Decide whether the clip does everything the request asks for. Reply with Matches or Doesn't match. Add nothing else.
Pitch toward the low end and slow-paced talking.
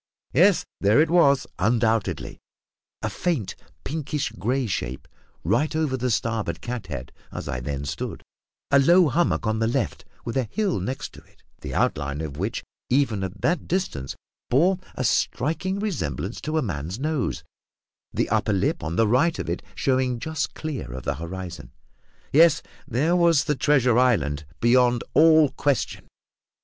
Doesn't match